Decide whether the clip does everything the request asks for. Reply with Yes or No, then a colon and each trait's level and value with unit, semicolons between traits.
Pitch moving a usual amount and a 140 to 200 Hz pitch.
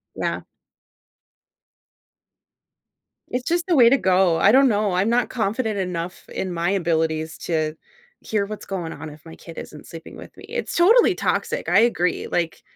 No: wide, 6.1 semitones; high, 190 Hz